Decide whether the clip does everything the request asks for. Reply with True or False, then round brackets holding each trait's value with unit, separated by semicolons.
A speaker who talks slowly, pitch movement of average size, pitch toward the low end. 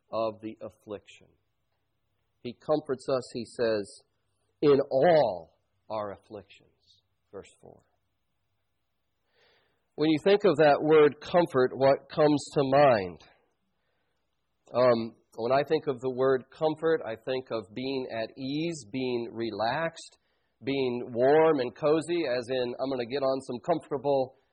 True (130 wpm; 4.6 semitones; 130 Hz)